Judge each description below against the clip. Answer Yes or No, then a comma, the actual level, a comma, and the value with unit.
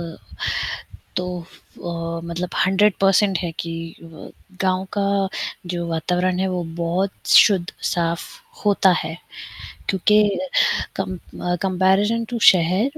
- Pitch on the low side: No, medium, 185 Hz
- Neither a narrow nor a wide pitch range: No, narrow, 2.3 semitones